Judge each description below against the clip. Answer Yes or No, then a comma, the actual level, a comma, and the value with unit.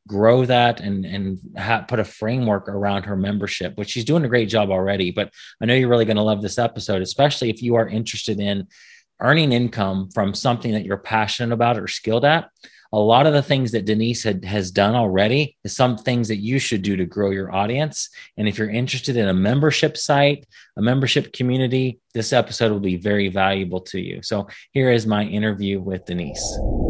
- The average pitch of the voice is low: Yes, low, 110 Hz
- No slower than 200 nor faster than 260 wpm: Yes, fast, 205 wpm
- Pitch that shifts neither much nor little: Yes, average, 3.6 semitones